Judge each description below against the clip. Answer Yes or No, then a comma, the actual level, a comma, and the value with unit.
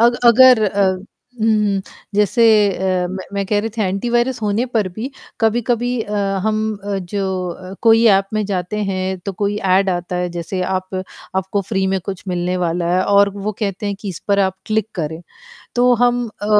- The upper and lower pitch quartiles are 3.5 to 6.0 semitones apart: No, average, 2.9 semitones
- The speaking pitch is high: Yes, high, 200 Hz